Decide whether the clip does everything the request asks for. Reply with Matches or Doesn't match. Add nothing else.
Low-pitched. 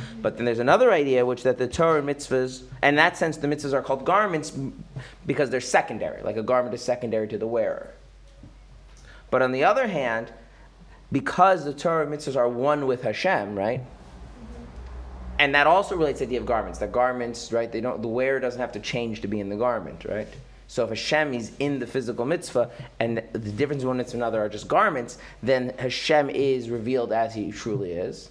Matches